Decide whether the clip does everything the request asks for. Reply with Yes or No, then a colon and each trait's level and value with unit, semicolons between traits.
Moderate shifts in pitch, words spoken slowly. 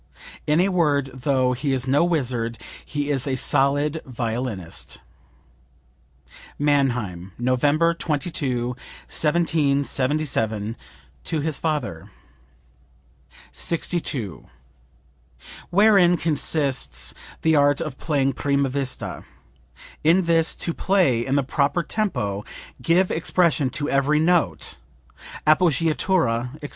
Yes: average, 4.1 semitones; slow, 100 wpm